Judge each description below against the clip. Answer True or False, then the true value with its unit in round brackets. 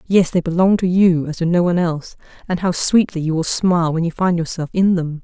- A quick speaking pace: True (250 wpm)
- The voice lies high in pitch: False (170 Hz)